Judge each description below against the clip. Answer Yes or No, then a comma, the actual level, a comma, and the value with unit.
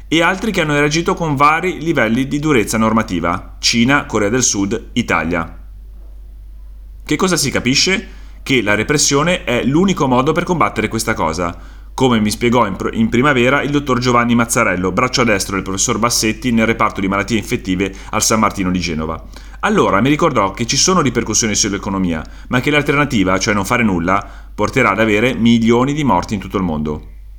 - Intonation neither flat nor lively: No, wide, 6.0 semitones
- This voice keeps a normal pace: No, fast, 175 wpm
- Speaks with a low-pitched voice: Yes, low, 115 Hz